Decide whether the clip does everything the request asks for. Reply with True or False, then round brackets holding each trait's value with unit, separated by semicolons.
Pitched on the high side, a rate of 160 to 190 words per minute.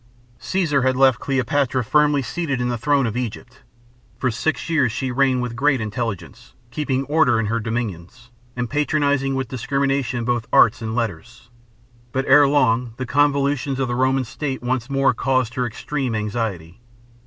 False (130 Hz; 165 wpm)